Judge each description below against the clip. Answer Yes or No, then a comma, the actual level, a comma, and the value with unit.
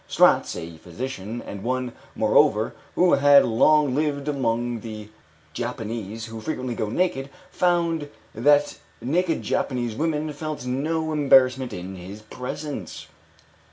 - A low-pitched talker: Yes, low, 130 Hz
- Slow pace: Yes, slow, 120 wpm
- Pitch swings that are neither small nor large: Yes, average, 5.0 semitones